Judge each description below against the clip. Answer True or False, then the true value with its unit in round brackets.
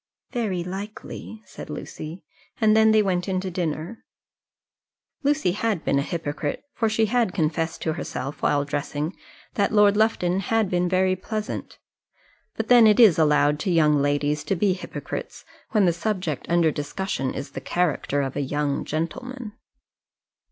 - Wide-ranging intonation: True (5.9 semitones)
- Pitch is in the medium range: True (180 Hz)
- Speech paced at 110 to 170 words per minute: True (160 wpm)